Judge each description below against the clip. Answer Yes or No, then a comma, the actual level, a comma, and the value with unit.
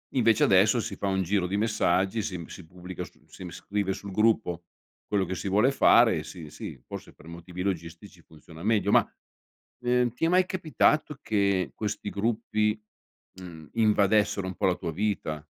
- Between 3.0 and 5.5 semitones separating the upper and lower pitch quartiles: Yes, average, 3.4 semitones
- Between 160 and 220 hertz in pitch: No, low, 100 Hz